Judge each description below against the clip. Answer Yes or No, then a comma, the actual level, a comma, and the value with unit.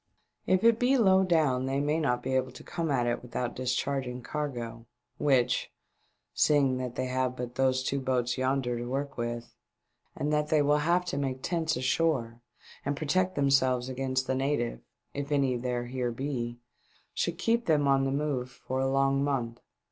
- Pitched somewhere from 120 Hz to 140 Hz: Yes, low, 135 Hz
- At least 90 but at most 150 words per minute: No, average, 185 wpm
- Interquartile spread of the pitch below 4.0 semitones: Yes, average, 2.8 semitones